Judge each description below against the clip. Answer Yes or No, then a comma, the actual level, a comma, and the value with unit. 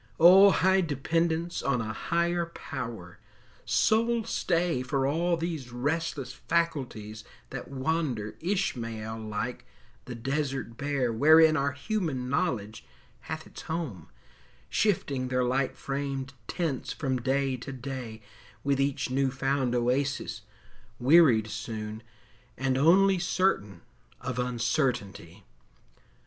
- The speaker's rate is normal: No, slow, 110 wpm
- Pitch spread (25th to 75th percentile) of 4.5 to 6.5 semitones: Yes, average, 5.1 semitones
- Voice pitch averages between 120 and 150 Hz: Yes, low, 135 Hz